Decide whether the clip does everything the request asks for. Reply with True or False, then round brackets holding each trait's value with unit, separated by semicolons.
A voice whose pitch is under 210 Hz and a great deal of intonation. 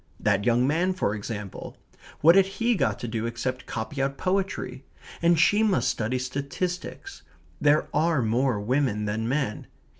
True (135 Hz; 7.1 semitones)